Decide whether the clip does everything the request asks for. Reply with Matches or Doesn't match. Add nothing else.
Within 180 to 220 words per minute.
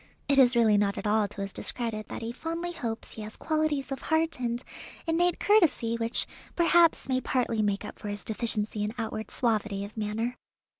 Matches